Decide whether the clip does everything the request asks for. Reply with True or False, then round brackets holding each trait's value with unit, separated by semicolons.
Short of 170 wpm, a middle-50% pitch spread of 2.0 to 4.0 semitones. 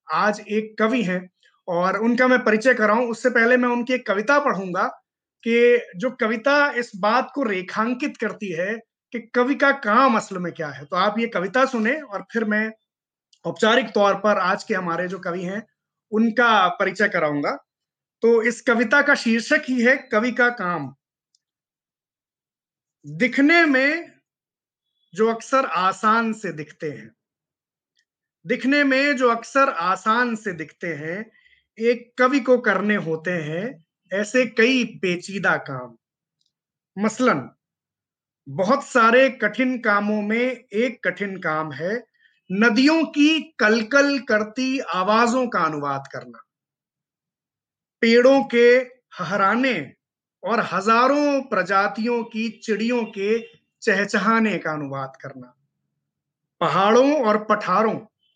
False (125 wpm; 5.0 semitones)